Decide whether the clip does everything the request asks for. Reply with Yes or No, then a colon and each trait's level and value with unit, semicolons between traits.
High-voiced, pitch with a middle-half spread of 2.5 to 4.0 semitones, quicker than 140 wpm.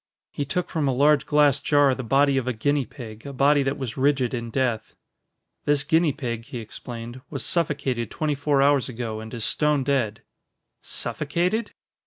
No: low, 135 Hz; average, 3.3 semitones; average, 180 wpm